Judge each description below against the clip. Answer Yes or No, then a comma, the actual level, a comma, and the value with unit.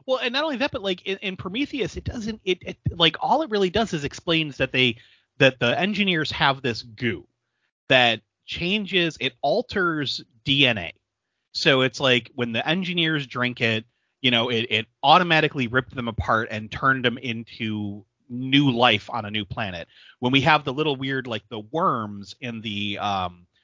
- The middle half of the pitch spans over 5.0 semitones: Yes, wide, 5.5 semitones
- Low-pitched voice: Yes, low, 130 Hz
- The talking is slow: No, average, 185 wpm